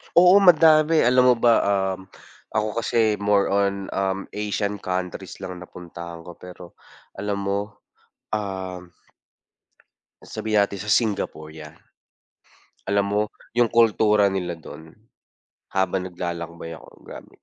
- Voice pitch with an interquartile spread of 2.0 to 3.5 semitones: Yes, average, 2.8 semitones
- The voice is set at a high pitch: No, low, 100 Hz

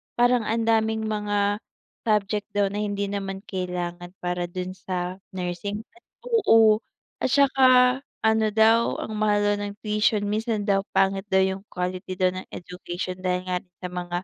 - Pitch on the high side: Yes, high, 205 Hz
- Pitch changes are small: No, average, 3.1 semitones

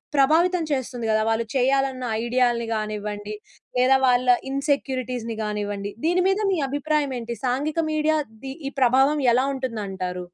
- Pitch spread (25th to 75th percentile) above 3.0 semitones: Yes, average, 3.7 semitones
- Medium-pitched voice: No, very high, 255 Hz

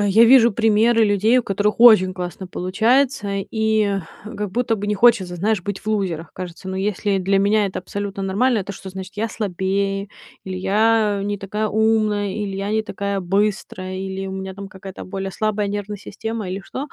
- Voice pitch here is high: Yes, high, 200 Hz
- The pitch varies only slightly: Yes, narrow, 2.1 semitones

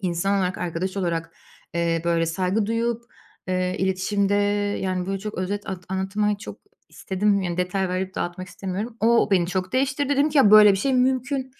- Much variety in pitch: No, average, 2.8 semitones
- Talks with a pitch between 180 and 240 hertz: Yes, high, 195 Hz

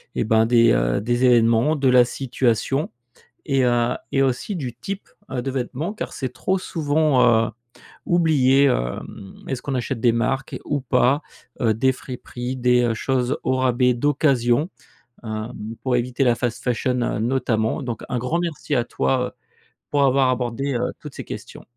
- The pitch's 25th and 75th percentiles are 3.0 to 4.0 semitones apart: No, narrow, 2.4 semitones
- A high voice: No, low, 125 Hz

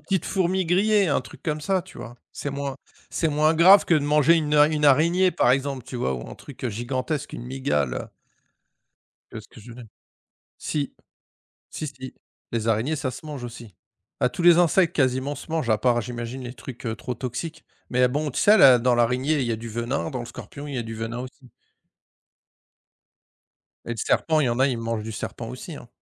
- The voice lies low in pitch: Yes, low, 130 Hz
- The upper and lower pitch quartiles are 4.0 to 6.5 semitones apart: Yes, average, 4.3 semitones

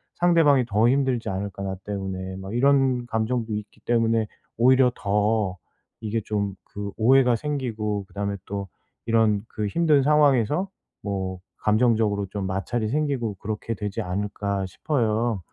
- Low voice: Yes, low, 110 Hz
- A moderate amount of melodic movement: Yes, average, 3.7 semitones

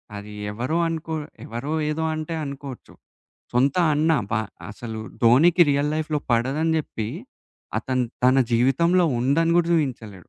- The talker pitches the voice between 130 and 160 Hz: Yes, medium, 140 Hz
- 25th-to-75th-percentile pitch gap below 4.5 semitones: No, average, 4.9 semitones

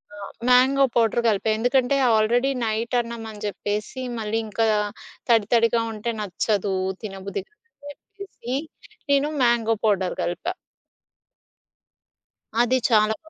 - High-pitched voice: Yes, high, 225 Hz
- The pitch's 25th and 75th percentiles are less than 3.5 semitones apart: Yes, average, 2.8 semitones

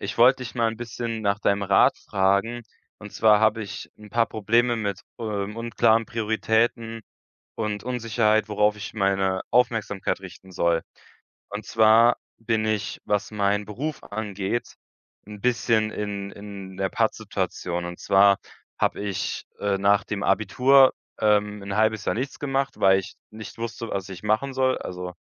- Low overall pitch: Yes, low, 105 Hz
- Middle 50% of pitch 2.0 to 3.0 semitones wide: Yes, narrow, 2.5 semitones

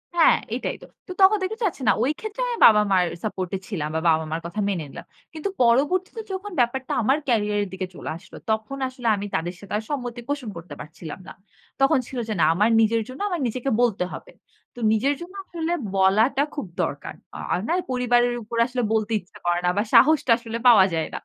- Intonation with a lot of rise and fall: Yes, wide, 6.2 semitones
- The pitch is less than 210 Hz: No, high, 235 Hz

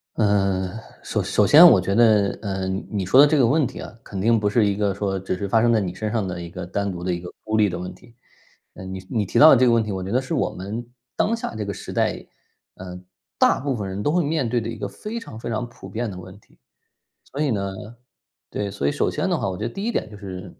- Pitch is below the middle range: Yes, low, 105 Hz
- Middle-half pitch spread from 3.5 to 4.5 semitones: Yes, average, 3.9 semitones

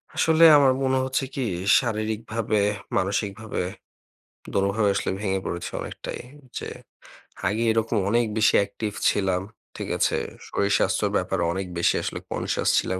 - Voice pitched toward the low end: Yes, low, 105 Hz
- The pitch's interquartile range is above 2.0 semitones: Yes, narrow, 2.6 semitones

